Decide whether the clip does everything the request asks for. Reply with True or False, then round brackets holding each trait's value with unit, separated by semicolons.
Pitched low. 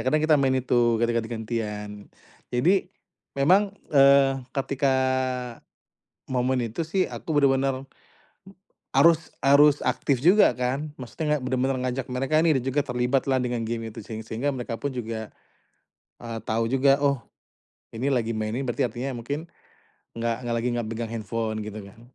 True (130 Hz)